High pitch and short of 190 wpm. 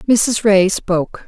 Yes: high, 205 Hz; average, 140 wpm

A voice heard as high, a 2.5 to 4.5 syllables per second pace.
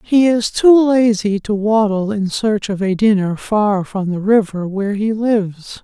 Yes: high, 210 Hz; 4.2 syllables/s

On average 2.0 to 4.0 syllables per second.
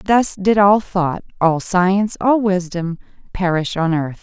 Yes: 3.9 syllables/s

